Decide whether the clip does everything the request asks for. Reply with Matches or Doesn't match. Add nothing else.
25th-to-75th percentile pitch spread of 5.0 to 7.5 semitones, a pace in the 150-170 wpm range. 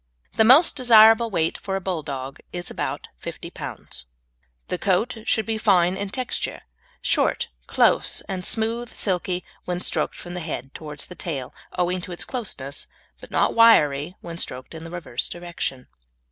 Matches